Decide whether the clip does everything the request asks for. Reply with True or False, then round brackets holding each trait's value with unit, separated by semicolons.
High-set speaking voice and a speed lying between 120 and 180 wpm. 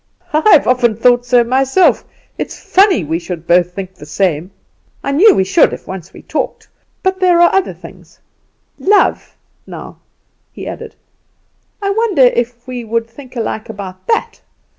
True (245 Hz; 160 wpm)